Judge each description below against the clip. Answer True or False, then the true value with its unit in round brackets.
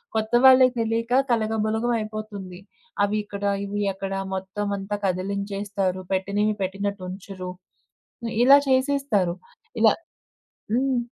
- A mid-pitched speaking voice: False (205 Hz)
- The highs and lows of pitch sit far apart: False (2.7 semitones)